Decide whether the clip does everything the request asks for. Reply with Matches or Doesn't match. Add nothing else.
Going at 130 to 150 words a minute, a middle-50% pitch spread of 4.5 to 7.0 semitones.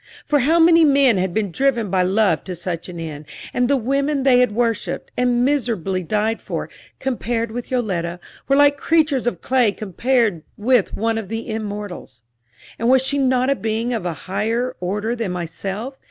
Doesn't match